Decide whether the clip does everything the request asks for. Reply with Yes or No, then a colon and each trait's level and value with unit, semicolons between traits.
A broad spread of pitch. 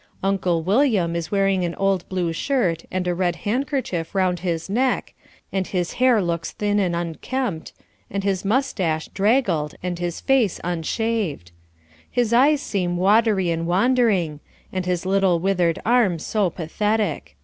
No: average, 4.1 semitones